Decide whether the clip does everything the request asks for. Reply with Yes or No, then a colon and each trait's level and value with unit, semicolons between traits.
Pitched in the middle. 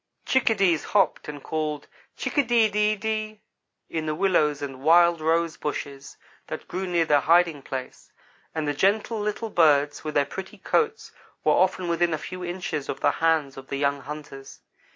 Yes: medium, 165 Hz